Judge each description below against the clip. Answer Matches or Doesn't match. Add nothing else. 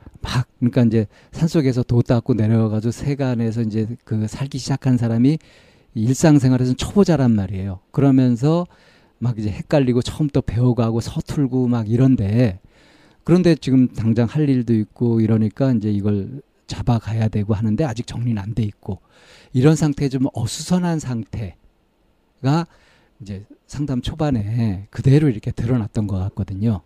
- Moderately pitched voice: Doesn't match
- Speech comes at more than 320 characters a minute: Matches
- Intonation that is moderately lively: Matches